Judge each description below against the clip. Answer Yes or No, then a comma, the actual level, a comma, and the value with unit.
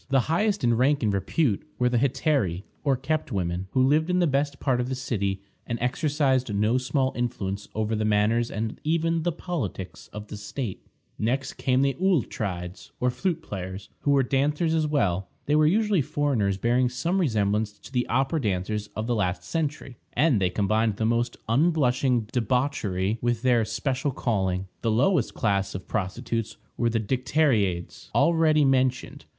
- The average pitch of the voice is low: Yes, low, 125 Hz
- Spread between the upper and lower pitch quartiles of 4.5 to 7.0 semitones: Yes, average, 5.3 semitones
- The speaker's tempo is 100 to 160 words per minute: No, average, 170 wpm